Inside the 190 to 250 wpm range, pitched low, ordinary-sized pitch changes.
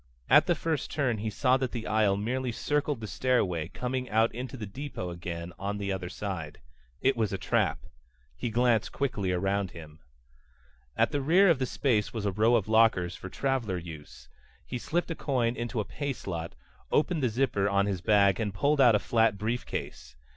Yes: average, 195 wpm; low, 110 Hz; average, 4.9 semitones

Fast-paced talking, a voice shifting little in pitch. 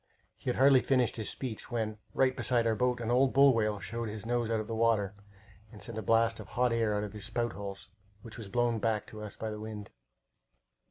Yes: fast, 235 wpm; narrow, 2.1 semitones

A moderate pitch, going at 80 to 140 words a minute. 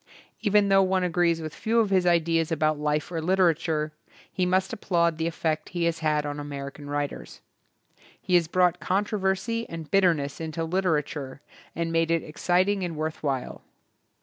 No: medium, 165 Hz; average, 175 wpm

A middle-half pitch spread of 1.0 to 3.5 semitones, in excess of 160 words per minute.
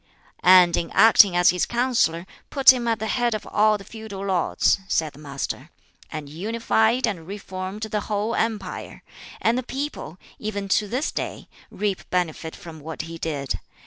No: average, 4.6 semitones; average, 170 wpm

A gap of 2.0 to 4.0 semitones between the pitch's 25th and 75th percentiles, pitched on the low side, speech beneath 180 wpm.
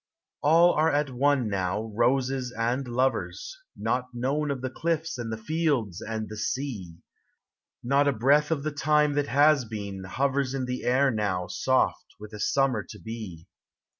No: average, 4.5 semitones; low, 130 Hz; average, 165 wpm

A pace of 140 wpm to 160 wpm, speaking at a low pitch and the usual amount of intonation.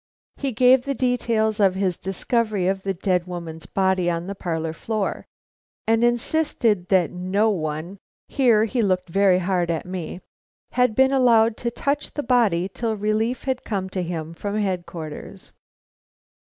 No: average, 155 wpm; high, 200 Hz; average, 4.4 semitones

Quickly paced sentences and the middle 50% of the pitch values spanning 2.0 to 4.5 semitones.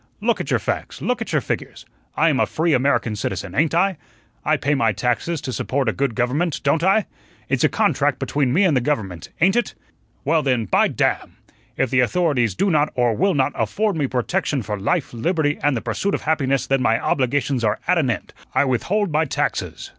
No: fast, 215 wpm; average, 5.1 semitones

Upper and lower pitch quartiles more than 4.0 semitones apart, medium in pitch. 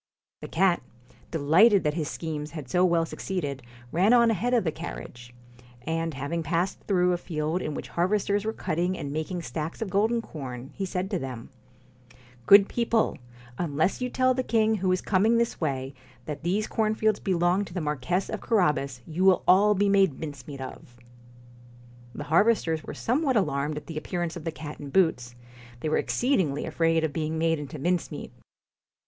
Yes: average, 4.8 semitones; medium, 170 Hz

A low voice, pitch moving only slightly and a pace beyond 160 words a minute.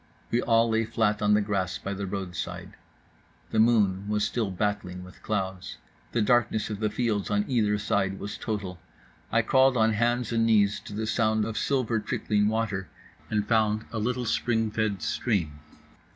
Yes: low, 105 Hz; narrow, 2.0 semitones; average, 175 wpm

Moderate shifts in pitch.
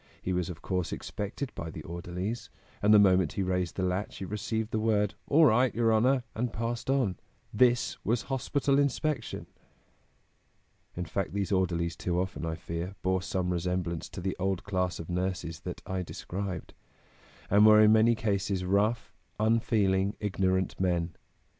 Yes: average, 3.5 semitones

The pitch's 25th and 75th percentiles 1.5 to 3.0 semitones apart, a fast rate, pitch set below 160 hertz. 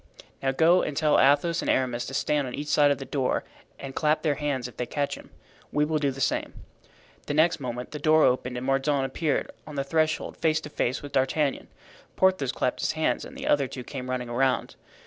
Yes: narrow, 2.6 semitones; fast, 225 wpm; medium, 140 Hz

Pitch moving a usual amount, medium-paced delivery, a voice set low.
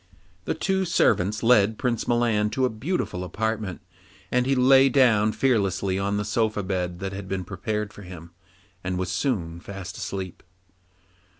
Yes: average, 4.2 semitones; average, 160 wpm; low, 105 Hz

